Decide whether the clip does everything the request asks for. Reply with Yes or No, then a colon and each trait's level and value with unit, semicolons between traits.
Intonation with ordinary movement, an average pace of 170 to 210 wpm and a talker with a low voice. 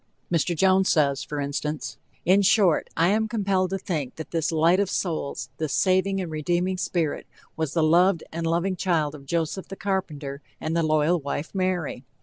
No: average, 3.4 semitones; average, 180 wpm; medium, 170 Hz